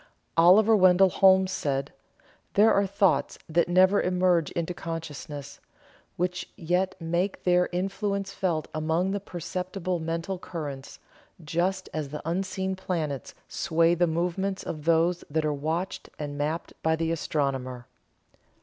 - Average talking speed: No, slow, 130 wpm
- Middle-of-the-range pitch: Yes, medium, 175 Hz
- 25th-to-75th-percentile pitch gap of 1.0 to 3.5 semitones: Yes, average, 2.9 semitones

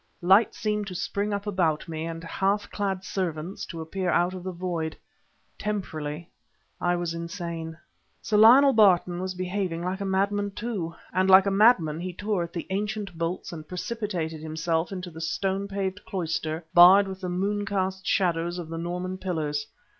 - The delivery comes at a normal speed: Yes, average, 175 wpm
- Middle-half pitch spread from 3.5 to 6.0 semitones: No, average, 3.0 semitones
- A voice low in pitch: No, medium, 185 Hz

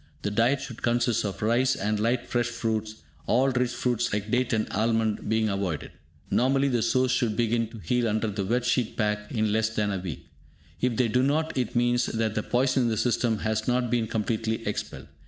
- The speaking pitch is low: Yes, low, 115 Hz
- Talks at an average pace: No, fast, 210 wpm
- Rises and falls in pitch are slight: Yes, narrow, 2.3 semitones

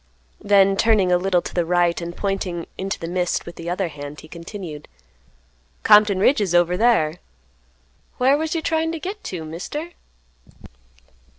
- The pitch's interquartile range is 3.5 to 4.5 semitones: Yes, average, 4.2 semitones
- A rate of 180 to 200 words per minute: No, average, 165 wpm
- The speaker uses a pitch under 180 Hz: No, medium, 185 Hz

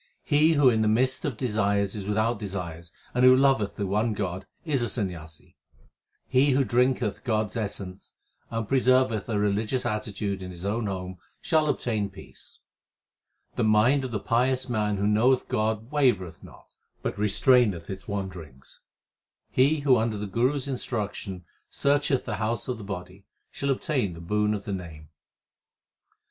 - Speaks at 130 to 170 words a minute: Yes, average, 165 wpm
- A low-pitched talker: Yes, low, 110 Hz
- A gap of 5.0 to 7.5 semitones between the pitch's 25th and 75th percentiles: No, average, 4.5 semitones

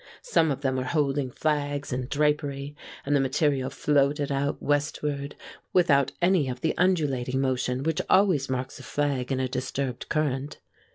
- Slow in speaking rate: No, average, 160 wpm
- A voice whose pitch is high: No, medium, 140 Hz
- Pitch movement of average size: No, narrow, 2.1 semitones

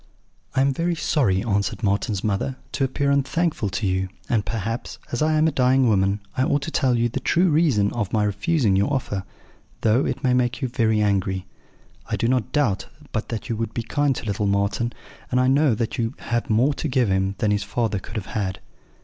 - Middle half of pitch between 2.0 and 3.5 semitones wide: No, average, 4.9 semitones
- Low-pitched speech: Yes, low, 115 Hz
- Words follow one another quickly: Yes, fast, 215 wpm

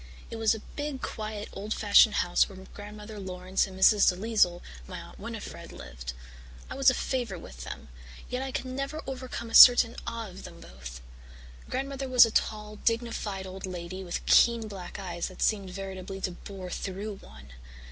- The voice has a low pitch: No, high, 205 Hz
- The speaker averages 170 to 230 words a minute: Yes, average, 175 wpm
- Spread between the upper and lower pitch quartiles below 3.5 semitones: No, average, 3.9 semitones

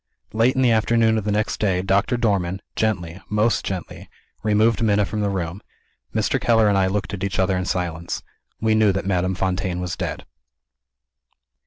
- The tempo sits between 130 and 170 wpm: No, average, 180 wpm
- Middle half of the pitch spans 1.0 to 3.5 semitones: Yes, average, 2.9 semitones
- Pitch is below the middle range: Yes, low, 100 Hz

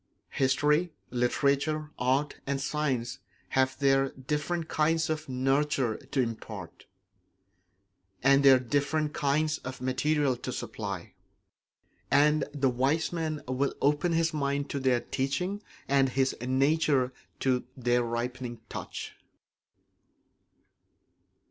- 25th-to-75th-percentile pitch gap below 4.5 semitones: Yes, average, 2.7 semitones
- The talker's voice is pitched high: No, medium, 140 Hz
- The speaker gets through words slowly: Yes, slow, 110 wpm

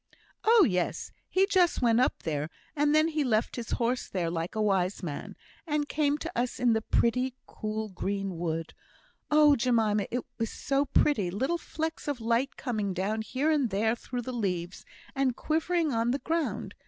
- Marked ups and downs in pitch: Yes, wide, 6.3 semitones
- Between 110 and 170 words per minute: No, average, 180 wpm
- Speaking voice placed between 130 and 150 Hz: No, high, 240 Hz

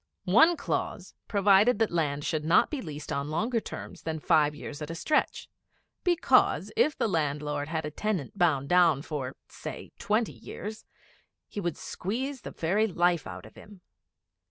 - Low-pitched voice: No, medium, 170 Hz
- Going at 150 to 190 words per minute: Yes, average, 165 wpm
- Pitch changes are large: Yes, wide, 6.1 semitones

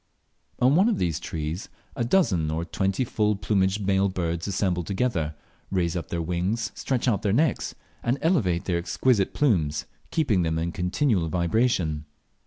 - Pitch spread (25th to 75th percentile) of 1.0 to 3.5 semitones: No, wide, 5.5 semitones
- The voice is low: Yes, very low, 95 Hz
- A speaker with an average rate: Yes, average, 165 wpm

